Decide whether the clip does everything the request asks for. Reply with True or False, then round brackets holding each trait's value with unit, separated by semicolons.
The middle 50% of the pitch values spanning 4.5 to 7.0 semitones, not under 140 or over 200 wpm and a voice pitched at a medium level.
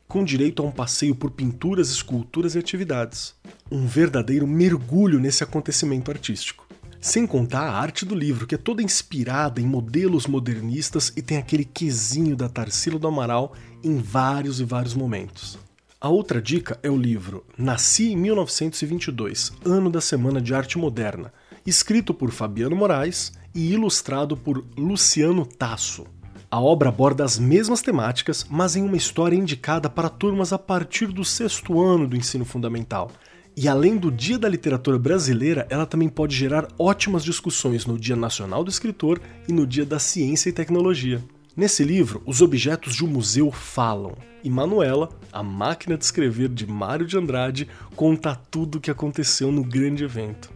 True (5.4 semitones; 165 wpm; 145 Hz)